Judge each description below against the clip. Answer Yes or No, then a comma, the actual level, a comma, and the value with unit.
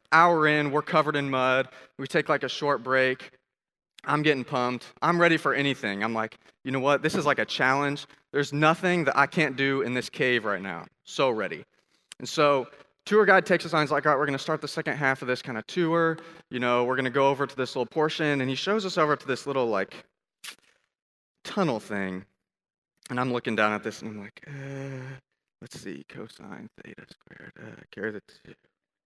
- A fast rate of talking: Yes, fast, 220 wpm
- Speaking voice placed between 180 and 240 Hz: No, low, 135 Hz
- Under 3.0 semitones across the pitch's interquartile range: No, average, 3.5 semitones